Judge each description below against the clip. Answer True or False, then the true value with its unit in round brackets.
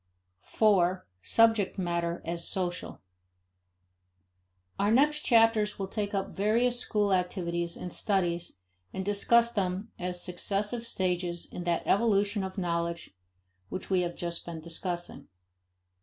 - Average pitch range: True (3.3 semitones)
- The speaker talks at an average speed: False (125 wpm)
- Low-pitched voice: False (190 Hz)